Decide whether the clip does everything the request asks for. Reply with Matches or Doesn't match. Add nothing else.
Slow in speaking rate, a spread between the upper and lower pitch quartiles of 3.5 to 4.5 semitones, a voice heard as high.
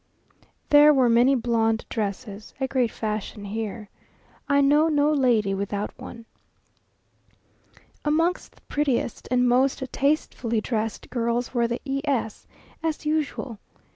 Matches